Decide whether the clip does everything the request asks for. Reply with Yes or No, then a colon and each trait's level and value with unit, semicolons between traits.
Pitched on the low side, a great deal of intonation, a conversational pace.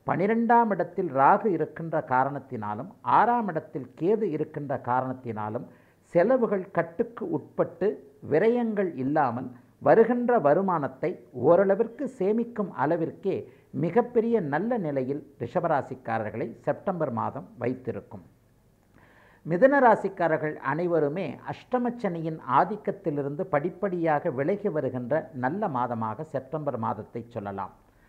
No: medium, 155 Hz; wide, 7.8 semitones; average, 85 wpm